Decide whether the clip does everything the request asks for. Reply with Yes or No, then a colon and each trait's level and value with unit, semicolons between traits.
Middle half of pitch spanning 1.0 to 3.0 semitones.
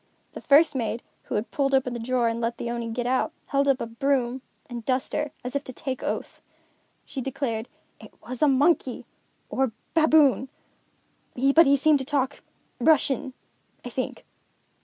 Yes: narrow, 2.6 semitones